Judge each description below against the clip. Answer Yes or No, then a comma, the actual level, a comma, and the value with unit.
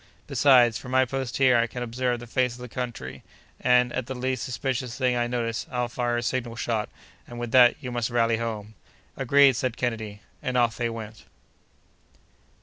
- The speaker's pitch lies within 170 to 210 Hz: No, low, 120 Hz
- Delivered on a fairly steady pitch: Yes, narrow, 1.6 semitones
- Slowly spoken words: No, average, 190 wpm